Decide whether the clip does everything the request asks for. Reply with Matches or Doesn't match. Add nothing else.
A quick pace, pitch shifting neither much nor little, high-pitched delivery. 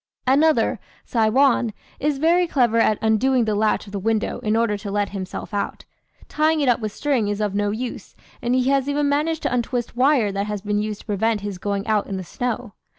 Matches